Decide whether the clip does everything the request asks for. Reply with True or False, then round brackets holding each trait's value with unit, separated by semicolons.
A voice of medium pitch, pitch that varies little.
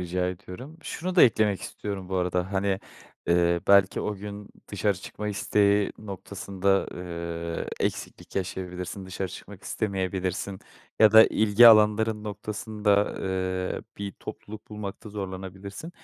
False (100 Hz; 2.2 semitones)